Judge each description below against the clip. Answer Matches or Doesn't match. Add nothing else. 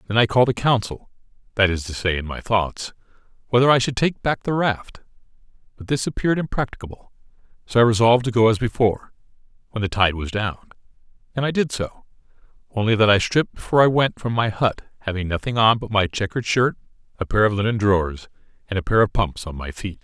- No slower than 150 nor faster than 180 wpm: Doesn't match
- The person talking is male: Matches